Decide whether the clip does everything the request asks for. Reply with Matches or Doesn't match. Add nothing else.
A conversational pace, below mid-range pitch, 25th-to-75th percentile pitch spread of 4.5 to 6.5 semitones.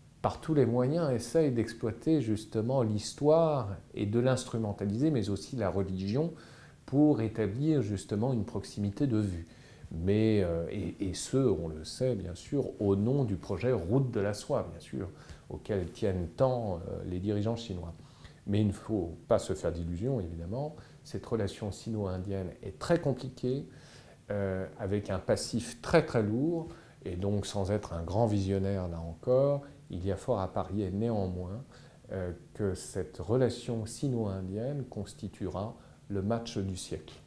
Matches